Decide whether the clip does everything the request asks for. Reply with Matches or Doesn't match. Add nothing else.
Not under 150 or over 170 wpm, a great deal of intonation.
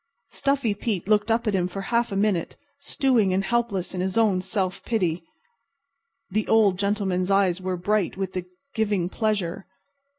Doesn't match